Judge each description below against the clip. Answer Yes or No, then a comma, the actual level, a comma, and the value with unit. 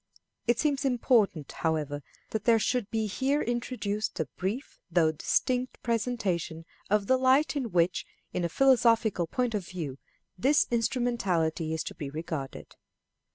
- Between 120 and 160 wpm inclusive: Yes, average, 145 wpm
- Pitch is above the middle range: Yes, high, 215 Hz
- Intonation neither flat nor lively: No, wide, 6.9 semitones